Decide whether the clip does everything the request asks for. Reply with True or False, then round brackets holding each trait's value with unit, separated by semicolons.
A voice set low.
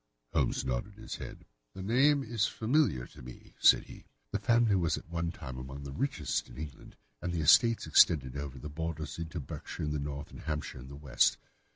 True (80 Hz)